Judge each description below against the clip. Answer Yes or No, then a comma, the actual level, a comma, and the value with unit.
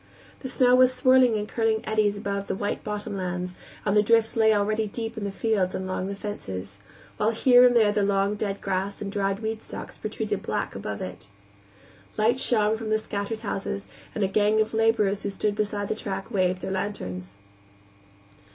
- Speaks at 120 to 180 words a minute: No, average, 195 wpm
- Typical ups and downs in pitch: No, narrow, 2.0 semitones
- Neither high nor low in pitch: No, high, 210 Hz